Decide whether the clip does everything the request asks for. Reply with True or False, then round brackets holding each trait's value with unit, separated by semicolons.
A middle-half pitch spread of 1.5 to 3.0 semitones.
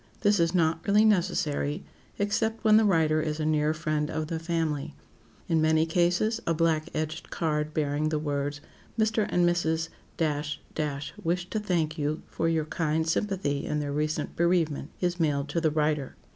True (2.4 semitones)